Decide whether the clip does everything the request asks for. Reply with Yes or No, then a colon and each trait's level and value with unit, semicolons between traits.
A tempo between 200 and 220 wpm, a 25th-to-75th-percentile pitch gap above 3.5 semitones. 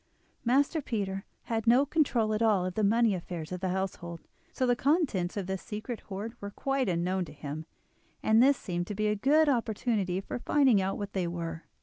Yes: fast, 205 wpm; average, 4.7 semitones